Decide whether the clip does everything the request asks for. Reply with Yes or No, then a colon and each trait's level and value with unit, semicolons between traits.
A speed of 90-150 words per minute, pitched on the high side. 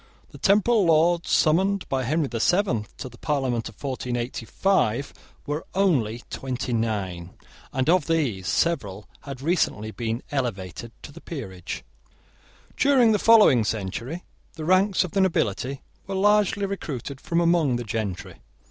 No: average, 140 wpm; medium, 140 Hz